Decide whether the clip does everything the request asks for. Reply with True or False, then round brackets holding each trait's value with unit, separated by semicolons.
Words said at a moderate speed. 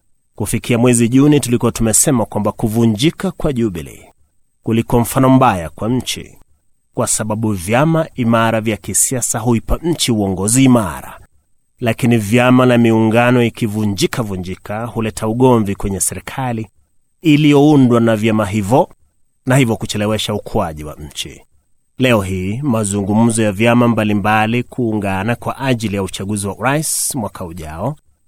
True (130 wpm)